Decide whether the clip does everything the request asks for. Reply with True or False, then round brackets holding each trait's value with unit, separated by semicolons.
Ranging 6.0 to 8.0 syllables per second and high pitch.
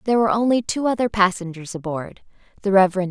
True (6.5 syllables/s; 200 Hz)